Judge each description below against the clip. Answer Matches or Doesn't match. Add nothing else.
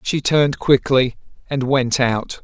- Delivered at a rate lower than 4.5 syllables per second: Matches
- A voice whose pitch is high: Doesn't match